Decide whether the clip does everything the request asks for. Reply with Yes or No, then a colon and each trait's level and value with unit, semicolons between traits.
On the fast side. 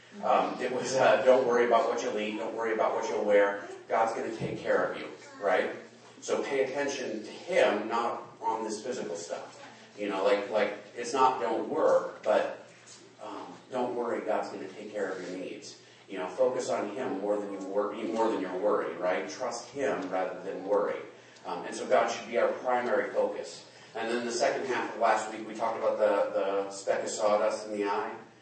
Yes: fast, 215 wpm